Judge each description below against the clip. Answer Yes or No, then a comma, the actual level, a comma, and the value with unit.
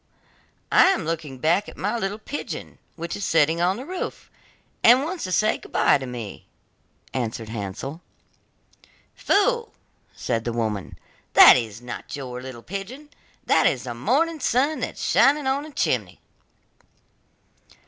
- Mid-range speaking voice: Yes, medium, 170 Hz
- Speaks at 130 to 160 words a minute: Yes, average, 150 wpm